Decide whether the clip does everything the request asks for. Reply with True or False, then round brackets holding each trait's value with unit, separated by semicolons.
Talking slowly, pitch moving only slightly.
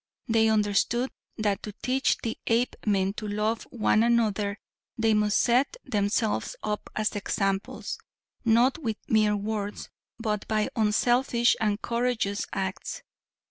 True (125 wpm; 2.2 semitones)